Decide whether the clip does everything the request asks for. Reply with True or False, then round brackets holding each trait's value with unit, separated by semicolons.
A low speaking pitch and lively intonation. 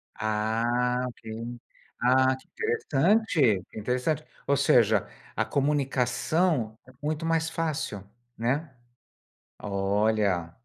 True (125 Hz; 6.0 semitones)